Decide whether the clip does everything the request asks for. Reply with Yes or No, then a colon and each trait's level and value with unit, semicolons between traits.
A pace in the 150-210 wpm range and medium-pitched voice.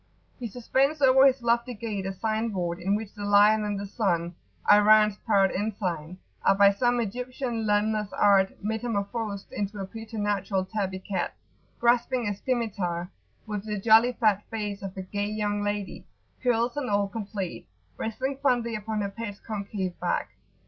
No: average, 160 wpm; high, 210 Hz